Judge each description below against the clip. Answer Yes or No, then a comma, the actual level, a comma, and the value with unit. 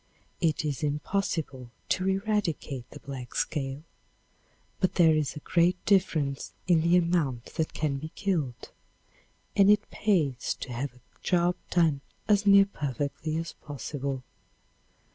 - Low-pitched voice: No, medium, 155 Hz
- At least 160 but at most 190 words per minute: No, slow, 135 wpm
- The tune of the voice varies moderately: Yes, average, 4.7 semitones